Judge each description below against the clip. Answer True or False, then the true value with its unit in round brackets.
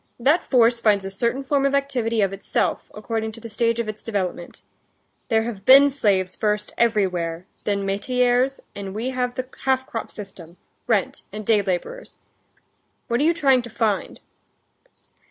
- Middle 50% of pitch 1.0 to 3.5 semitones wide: False (4.1 semitones)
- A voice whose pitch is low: False (225 Hz)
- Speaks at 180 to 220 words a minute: False (165 wpm)